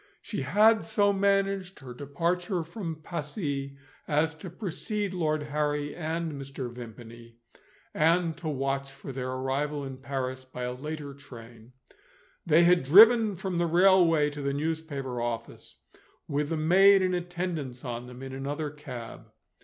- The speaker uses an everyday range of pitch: Yes, average, 4.7 semitones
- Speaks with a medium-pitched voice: Yes, medium, 150 Hz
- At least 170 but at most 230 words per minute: No, average, 145 wpm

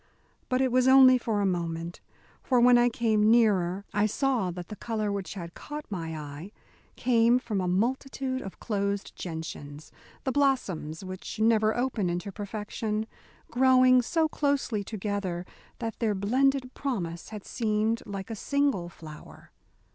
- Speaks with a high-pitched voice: Yes, high, 215 Hz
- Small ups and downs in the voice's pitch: No, average, 5.1 semitones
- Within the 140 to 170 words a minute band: Yes, average, 150 wpm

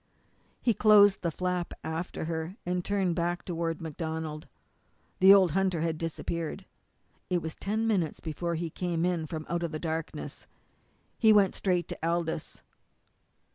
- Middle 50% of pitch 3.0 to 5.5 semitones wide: No, narrow, 2.4 semitones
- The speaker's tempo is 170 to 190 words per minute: No, average, 150 wpm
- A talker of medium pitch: Yes, medium, 170 Hz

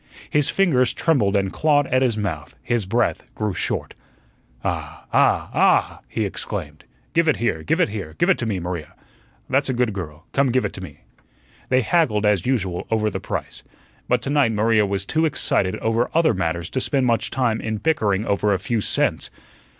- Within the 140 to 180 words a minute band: No, average, 195 wpm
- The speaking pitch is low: Yes, low, 110 Hz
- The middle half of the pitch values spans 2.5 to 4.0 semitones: No, average, 5.0 semitones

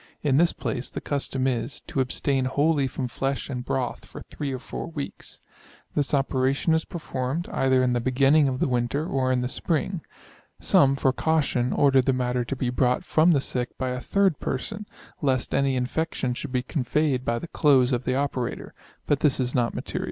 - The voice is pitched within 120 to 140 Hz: Yes, low, 135 Hz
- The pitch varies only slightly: Yes, narrow, 2.3 semitones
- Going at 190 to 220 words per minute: Yes, average, 195 wpm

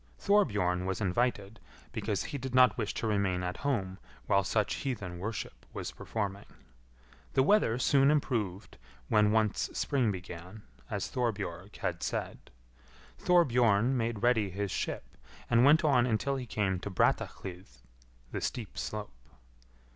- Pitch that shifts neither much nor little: Yes, average, 4.5 semitones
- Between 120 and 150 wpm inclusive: Yes, average, 140 wpm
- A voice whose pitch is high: No, low, 110 Hz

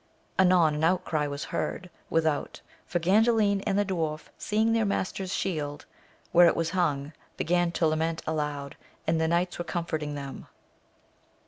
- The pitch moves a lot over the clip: No, average, 3.2 semitones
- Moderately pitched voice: Yes, medium, 165 Hz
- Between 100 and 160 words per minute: Yes, average, 150 wpm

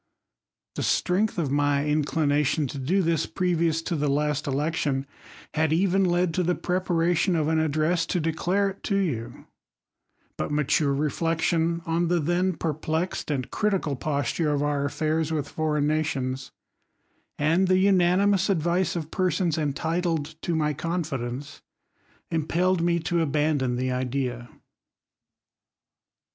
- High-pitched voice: No, medium, 160 Hz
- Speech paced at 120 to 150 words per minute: Yes, average, 140 wpm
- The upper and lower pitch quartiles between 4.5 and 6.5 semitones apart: No, average, 3.1 semitones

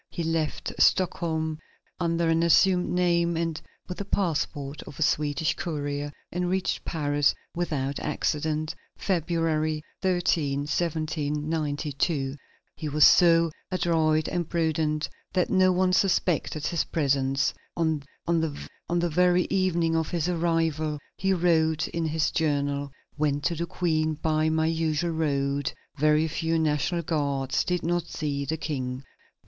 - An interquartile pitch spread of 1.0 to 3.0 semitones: Yes, narrow, 2.4 semitones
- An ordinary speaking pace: No, slow, 130 wpm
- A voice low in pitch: No, medium, 160 Hz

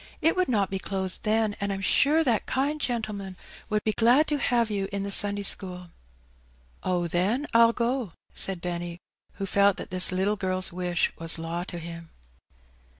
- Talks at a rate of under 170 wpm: No, average, 180 wpm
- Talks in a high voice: Yes, high, 200 Hz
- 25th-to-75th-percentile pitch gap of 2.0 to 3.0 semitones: No, average, 4.1 semitones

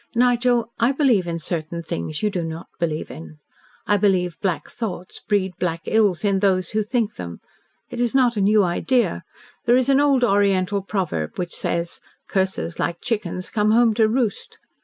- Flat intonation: No, average, 5.1 semitones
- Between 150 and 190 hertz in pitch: No, high, 200 Hz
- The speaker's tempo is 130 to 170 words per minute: No, average, 180 wpm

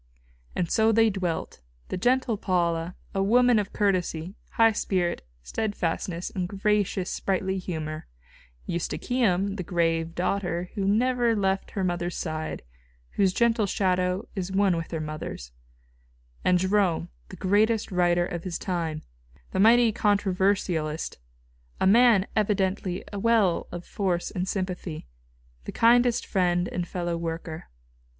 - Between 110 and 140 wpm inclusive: Yes, slow, 135 wpm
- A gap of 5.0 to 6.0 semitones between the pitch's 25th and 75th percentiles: No, average, 3.0 semitones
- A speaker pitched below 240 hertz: Yes, medium, 185 Hz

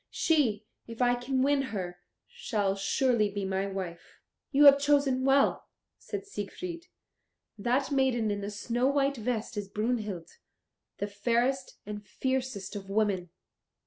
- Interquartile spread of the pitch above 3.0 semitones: Yes, average, 5.0 semitones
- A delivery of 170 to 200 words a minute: No, average, 140 wpm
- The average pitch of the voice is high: Yes, high, 235 Hz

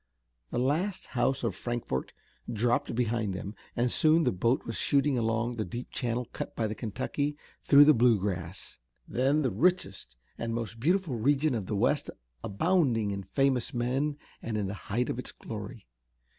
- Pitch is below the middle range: Yes, low, 120 Hz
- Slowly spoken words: No, average, 170 wpm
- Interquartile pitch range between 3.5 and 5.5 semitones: Yes, average, 4.3 semitones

